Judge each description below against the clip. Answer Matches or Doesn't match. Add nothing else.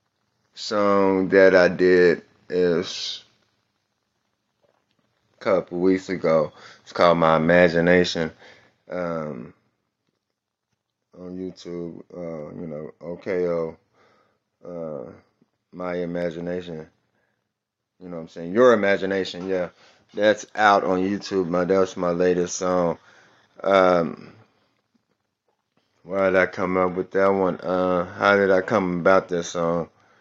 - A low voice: Matches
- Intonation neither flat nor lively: Doesn't match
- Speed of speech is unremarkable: Doesn't match